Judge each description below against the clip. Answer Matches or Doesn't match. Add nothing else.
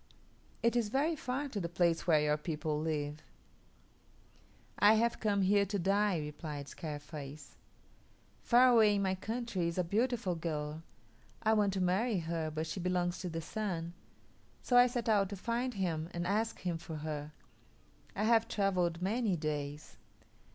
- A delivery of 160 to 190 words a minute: Matches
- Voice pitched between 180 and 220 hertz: Matches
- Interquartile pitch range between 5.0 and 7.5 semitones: Matches